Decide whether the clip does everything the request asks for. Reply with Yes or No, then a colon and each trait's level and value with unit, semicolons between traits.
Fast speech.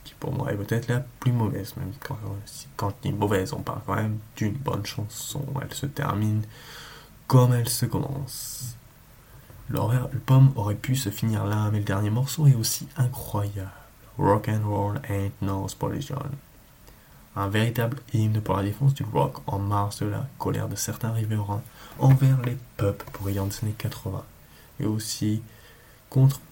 No: average, 170 wpm